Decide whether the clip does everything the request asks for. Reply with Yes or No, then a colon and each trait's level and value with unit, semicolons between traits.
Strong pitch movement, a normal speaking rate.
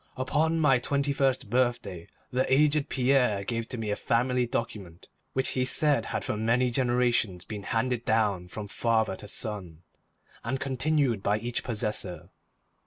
No: average, 3.7 semitones; average, 155 wpm